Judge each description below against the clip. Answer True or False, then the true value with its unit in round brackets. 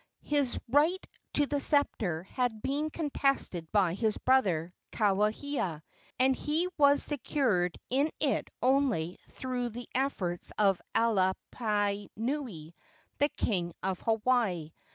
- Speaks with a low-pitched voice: False (230 Hz)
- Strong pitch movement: True (6.8 semitones)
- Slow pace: True (110 wpm)